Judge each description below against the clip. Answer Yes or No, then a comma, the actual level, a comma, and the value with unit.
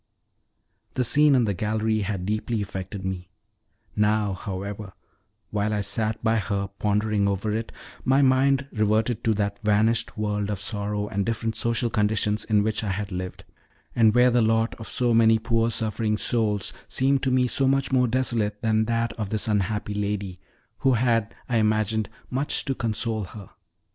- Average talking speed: Yes, average, 170 wpm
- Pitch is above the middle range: No, low, 110 Hz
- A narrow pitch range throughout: Yes, narrow, 2.0 semitones